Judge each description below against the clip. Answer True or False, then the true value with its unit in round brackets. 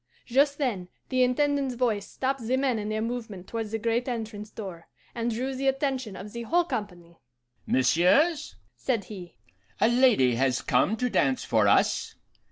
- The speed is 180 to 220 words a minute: False (170 wpm)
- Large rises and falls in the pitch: False (4.6 semitones)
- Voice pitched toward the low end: False (230 Hz)